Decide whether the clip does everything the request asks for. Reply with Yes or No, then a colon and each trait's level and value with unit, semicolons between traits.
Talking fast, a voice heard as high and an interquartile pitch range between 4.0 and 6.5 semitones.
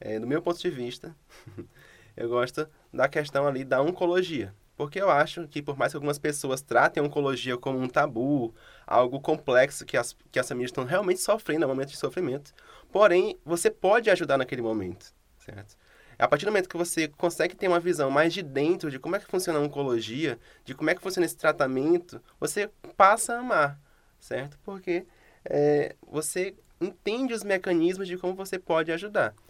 No: fast, 190 wpm; medium, 155 Hz; average, 5.2 semitones